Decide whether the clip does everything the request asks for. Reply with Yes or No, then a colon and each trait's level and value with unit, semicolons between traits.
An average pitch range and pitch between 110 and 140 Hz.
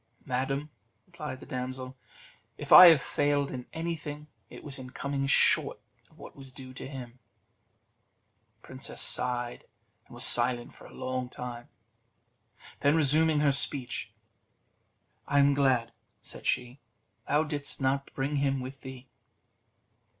No: narrow, 2.1 semitones; low, 135 Hz